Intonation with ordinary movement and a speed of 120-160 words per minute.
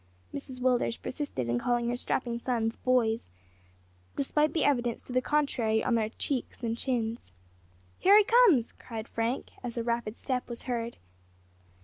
No: narrow, 2.3 semitones; average, 155 wpm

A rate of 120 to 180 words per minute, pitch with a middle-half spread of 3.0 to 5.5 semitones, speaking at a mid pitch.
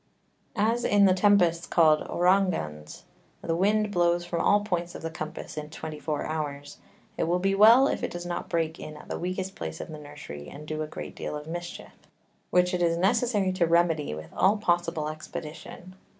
No: average, 195 wpm; average, 3.4 semitones; medium, 170 Hz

